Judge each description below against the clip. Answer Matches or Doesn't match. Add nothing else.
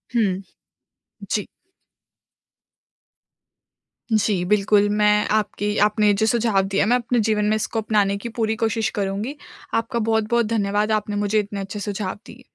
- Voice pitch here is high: Matches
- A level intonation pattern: Matches